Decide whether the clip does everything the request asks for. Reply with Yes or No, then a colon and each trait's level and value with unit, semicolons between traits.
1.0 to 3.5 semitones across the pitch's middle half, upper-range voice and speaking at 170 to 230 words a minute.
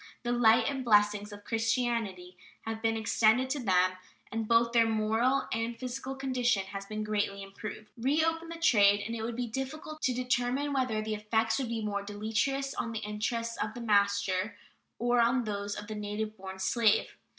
Yes: average, 2.9 semitones; high, 225 Hz; average, 185 wpm